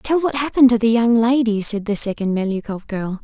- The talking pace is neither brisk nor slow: No, fast, 225 wpm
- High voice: Yes, high, 225 Hz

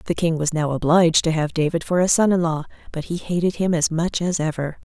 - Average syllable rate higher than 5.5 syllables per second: Yes, 5.9 syllables/s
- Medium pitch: Yes, medium, 165 Hz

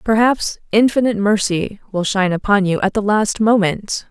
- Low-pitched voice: No, high, 205 Hz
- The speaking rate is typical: Yes, average, 160 wpm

